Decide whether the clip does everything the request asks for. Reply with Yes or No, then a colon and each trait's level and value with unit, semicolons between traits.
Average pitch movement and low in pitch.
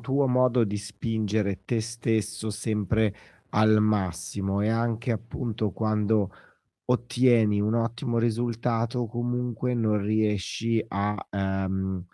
No: narrow, 2.3 semitones; low, 110 Hz